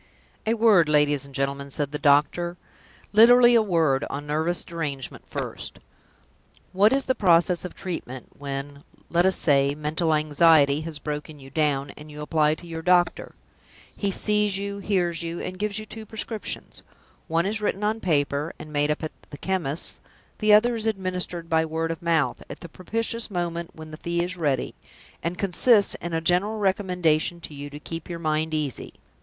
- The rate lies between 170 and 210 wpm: Yes, average, 180 wpm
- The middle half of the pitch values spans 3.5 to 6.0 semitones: Yes, average, 4.2 semitones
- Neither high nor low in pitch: Yes, medium, 165 Hz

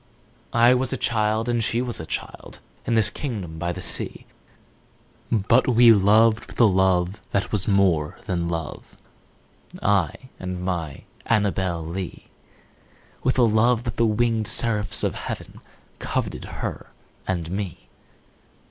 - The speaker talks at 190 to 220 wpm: No, average, 140 wpm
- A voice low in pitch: Yes, low, 105 Hz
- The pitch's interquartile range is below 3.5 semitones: No, average, 4.3 semitones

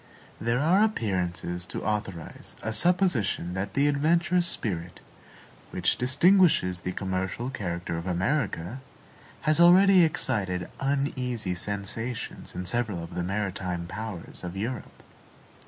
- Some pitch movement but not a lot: No, wide, 7.7 semitones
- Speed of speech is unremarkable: No, slow, 120 wpm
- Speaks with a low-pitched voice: Yes, low, 105 Hz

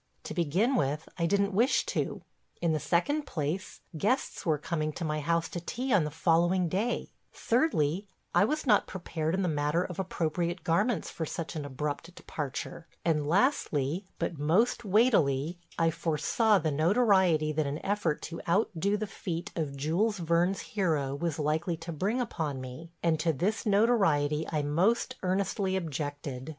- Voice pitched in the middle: Yes, medium, 170 Hz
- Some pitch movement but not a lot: Yes, average, 4.5 semitones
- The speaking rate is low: No, average, 165 wpm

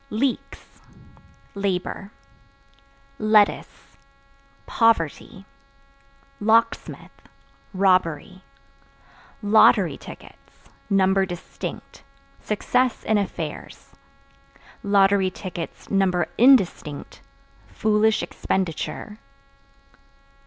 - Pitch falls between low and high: No, high, 200 Hz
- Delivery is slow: Yes, slow, 50 wpm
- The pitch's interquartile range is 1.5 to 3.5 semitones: Yes, average, 2.7 semitones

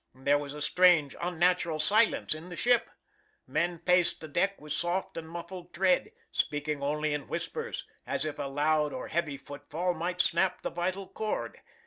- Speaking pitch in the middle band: Yes, medium, 170 Hz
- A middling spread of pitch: Yes, average, 3.3 semitones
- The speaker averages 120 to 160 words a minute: No, average, 170 wpm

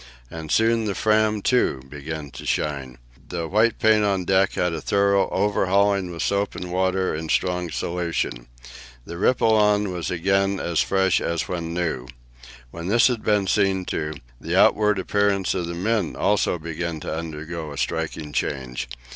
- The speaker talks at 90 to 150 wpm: No, average, 165 wpm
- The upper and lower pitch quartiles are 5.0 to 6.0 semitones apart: No, average, 3.8 semitones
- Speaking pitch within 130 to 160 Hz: No, very low, 90 Hz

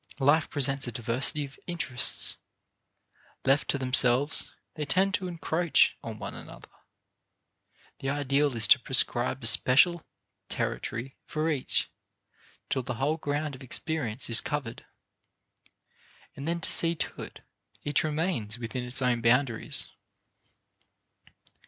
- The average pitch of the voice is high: No, low, 135 Hz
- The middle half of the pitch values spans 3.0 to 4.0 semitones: Yes, average, 3.7 semitones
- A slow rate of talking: Yes, slow, 125 wpm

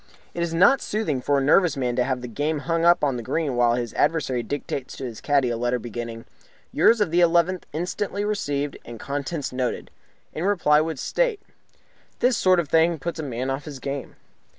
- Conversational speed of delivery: No, fast, 210 wpm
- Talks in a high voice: No, medium, 145 Hz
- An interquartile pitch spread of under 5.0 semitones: No, average, 5.3 semitones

